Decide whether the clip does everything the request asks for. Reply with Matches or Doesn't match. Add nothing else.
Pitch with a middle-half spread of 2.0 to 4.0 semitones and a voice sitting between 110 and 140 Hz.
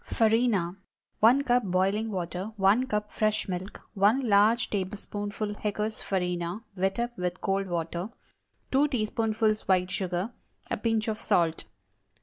Doesn't match